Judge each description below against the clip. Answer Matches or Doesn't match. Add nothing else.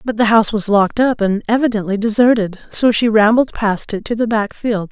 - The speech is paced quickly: Matches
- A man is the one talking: Doesn't match